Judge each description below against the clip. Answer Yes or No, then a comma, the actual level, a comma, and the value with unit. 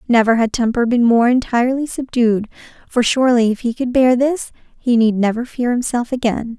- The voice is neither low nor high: No, high, 240 Hz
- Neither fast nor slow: Yes, average, 180 wpm